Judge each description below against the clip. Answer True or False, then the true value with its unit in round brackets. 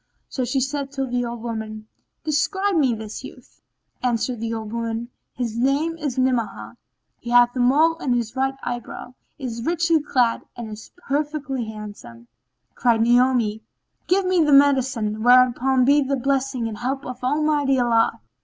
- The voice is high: True (250 Hz)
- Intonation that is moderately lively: True (3.3 semitones)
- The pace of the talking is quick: False (165 wpm)